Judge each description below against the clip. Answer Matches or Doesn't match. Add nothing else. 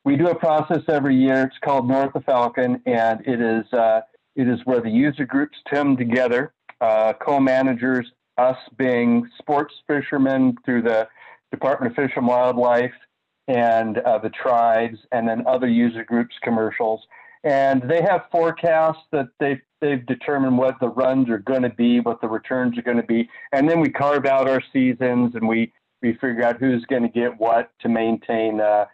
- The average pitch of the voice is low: Matches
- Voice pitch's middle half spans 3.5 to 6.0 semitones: Doesn't match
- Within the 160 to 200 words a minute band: Matches